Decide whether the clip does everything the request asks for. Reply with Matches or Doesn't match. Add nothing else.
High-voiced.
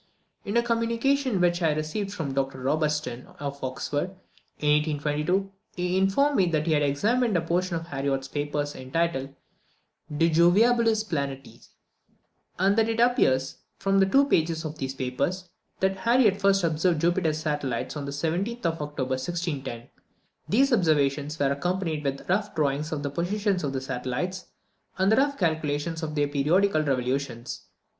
Doesn't match